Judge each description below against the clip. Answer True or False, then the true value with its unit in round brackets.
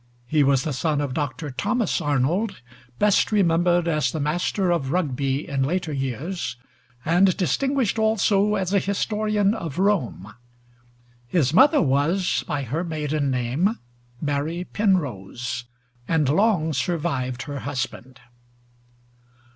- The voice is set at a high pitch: False (160 Hz)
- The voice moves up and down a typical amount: False (5.9 semitones)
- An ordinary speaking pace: False (125 wpm)